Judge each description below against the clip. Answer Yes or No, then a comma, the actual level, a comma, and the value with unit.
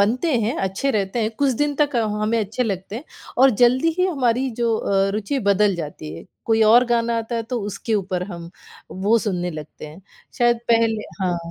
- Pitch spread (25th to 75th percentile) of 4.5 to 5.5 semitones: No, average, 4.0 semitones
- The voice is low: No, high, 225 Hz